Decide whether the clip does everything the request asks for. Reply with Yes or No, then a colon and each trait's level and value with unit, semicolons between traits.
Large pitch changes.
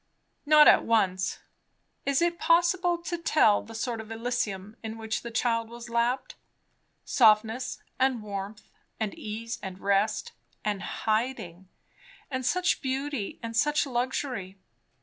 No: average, 3.8 semitones